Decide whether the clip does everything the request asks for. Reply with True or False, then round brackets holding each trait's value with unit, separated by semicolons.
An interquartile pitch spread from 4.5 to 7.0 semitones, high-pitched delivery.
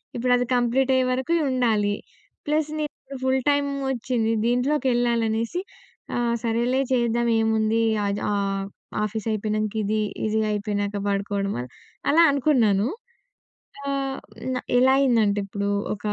False (3.6 semitones; 235 Hz)